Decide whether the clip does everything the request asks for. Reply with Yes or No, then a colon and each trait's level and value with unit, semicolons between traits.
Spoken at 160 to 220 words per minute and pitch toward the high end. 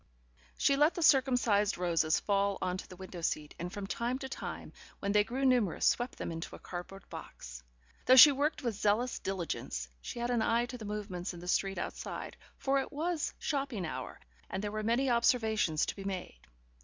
Yes: average, 200 wpm; high, 210 Hz